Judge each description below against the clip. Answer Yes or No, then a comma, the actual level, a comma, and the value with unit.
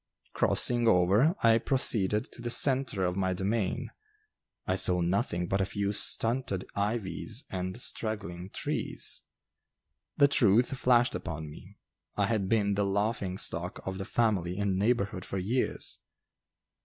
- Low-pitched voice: Yes, low, 100 Hz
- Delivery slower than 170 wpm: Yes, average, 140 wpm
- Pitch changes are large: No, average, 3.9 semitones